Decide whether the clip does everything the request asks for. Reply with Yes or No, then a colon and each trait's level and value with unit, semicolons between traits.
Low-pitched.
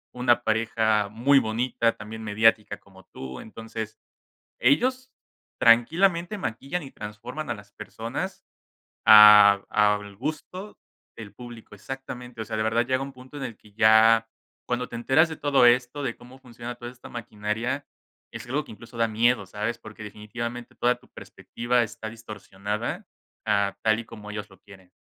Yes: low, 115 Hz